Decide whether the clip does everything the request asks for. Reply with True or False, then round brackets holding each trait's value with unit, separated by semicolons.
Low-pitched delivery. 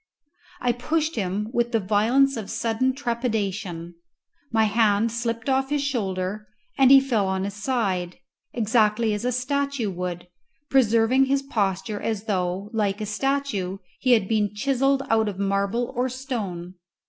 False (225 Hz)